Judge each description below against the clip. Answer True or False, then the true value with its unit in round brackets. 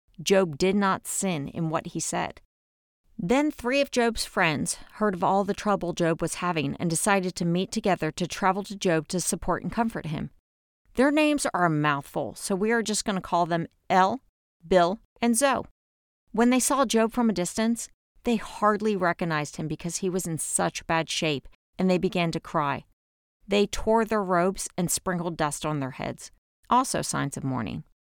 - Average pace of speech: True (190 wpm)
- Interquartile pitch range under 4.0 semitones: False (4.4 semitones)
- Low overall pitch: False (180 Hz)